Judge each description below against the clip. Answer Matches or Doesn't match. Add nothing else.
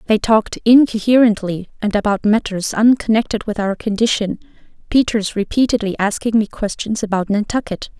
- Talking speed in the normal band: Doesn't match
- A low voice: Doesn't match